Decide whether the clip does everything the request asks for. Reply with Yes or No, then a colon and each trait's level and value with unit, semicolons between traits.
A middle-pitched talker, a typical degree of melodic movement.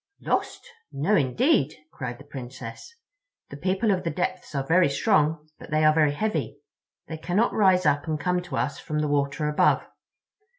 Yes: medium, 155 Hz; average, 4.2 semitones